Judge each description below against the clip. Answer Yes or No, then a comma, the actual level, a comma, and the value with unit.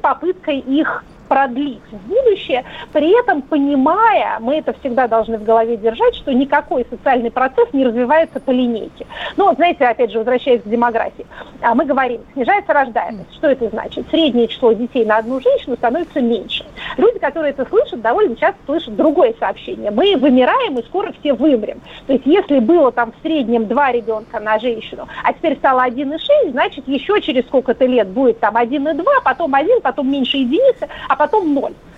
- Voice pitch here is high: Yes, very high, 275 Hz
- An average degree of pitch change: Yes, average, 4.5 semitones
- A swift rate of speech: Yes, fast, 170 wpm